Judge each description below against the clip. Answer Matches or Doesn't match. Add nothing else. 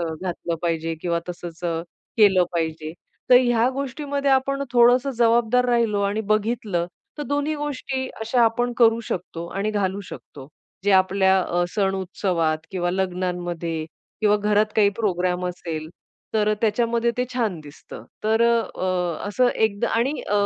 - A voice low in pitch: Doesn't match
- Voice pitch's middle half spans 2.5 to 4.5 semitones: Doesn't match